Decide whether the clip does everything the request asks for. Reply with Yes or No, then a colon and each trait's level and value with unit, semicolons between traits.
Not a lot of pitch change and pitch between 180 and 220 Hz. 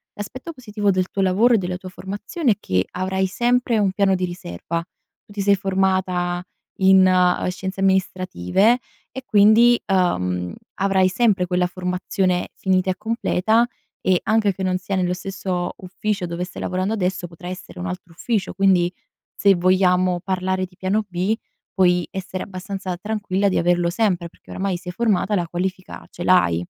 Yes: narrow, 1.8 semitones; medium, 185 Hz